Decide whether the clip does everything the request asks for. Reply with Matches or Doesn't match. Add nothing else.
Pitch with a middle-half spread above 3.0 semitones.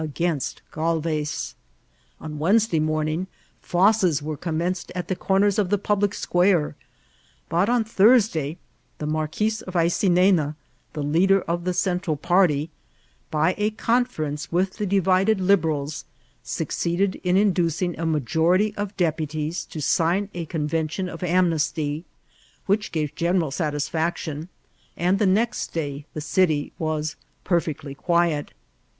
Matches